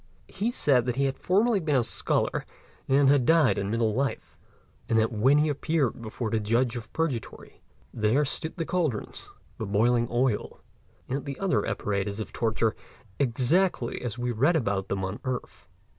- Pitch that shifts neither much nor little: Yes, average, 4.6 semitones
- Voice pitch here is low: Yes, low, 125 Hz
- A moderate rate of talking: Yes, average, 165 wpm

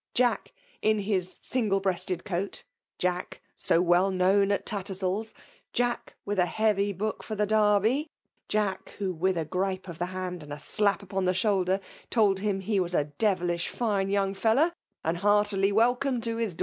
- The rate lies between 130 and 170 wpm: No, average, 180 wpm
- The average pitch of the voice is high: Yes, high, 195 Hz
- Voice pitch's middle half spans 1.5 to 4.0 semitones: Yes, narrow, 2.5 semitones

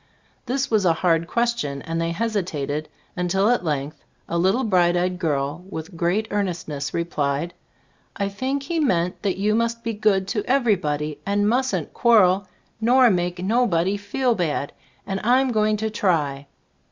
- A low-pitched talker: No, high, 190 Hz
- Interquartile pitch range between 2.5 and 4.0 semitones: No, average, 5.1 semitones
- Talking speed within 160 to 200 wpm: Yes, average, 165 wpm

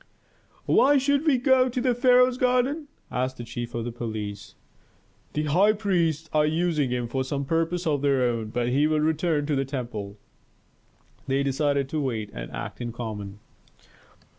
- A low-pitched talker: No, medium, 145 Hz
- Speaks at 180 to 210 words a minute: No, average, 165 wpm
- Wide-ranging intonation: Yes, wide, 7.2 semitones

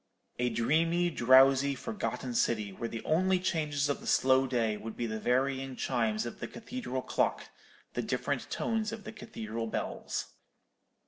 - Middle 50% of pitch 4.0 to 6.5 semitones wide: Yes, wide, 5.5 semitones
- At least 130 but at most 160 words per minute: Yes, average, 155 wpm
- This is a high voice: No, low, 130 Hz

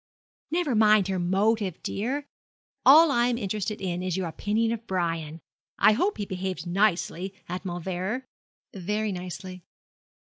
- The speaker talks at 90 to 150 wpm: Yes, average, 140 wpm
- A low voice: No, high, 195 Hz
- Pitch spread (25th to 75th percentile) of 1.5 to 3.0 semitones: No, average, 3.5 semitones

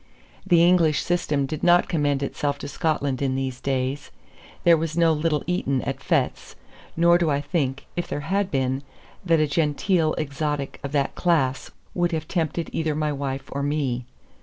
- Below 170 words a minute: No, average, 175 wpm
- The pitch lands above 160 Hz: No, medium, 150 Hz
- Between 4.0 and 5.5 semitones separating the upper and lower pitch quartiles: No, average, 3.2 semitones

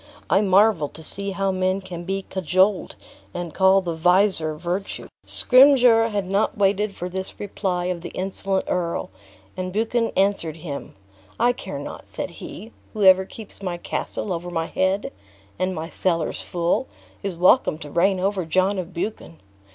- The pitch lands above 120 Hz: Yes, high, 190 Hz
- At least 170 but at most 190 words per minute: No, average, 160 wpm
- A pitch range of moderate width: No, narrow, 2.3 semitones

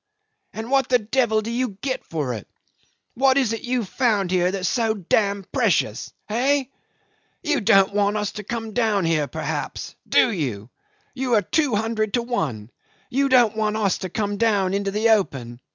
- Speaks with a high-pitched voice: Yes, high, 215 Hz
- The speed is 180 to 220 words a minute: Yes, average, 185 wpm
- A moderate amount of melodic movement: Yes, average, 3.9 semitones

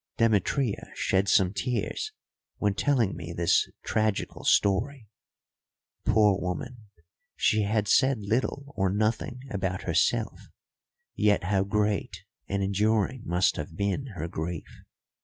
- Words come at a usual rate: No, slow, 120 wpm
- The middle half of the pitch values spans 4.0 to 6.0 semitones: No, average, 3.1 semitones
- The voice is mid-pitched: No, low, 100 Hz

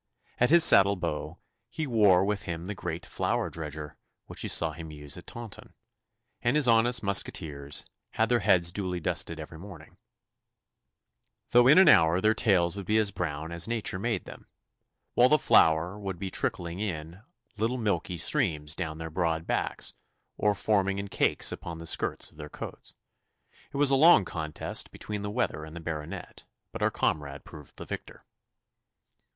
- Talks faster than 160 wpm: Yes, average, 175 wpm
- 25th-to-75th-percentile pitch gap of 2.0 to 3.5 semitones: No, average, 4.9 semitones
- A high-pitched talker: No, very low, 90 Hz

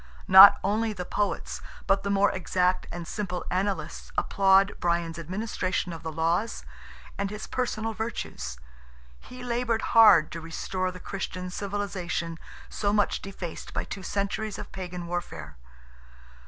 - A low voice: No, high, 190 Hz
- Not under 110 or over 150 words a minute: Yes, average, 140 wpm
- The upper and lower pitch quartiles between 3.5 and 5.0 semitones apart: No, average, 3.0 semitones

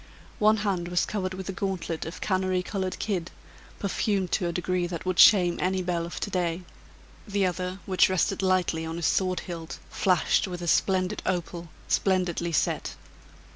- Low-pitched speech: No, medium, 185 Hz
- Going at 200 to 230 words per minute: No, average, 175 wpm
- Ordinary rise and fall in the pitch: No, narrow, 1.5 semitones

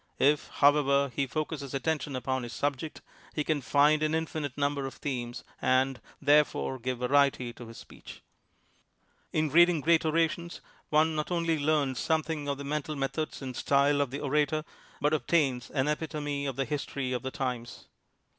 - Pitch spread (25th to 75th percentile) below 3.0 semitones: Yes, narrow, 2.5 semitones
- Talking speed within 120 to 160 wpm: No, average, 170 wpm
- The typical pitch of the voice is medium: Yes, medium, 145 Hz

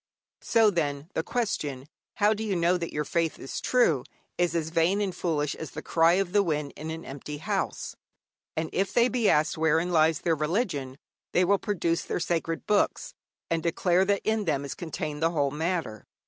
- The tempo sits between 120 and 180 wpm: No, average, 195 wpm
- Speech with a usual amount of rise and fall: Yes, average, 3.8 semitones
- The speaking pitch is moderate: Yes, medium, 165 Hz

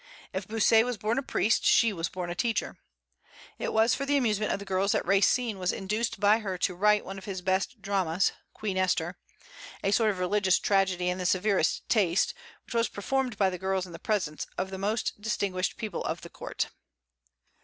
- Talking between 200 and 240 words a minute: Yes, fast, 205 wpm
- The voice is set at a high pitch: Yes, high, 195 Hz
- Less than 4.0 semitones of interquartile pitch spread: Yes, narrow, 2.6 semitones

